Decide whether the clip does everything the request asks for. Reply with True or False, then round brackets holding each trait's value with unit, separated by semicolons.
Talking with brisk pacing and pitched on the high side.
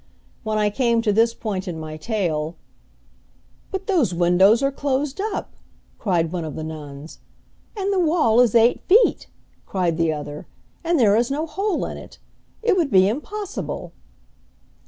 False (160 wpm; 220 Hz)